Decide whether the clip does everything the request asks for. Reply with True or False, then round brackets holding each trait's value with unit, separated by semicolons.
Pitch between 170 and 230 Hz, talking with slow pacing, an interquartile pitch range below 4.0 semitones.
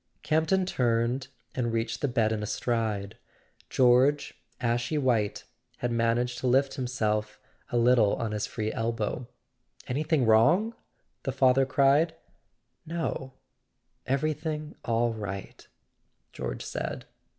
False (120 Hz; 115 wpm; 3.5 semitones)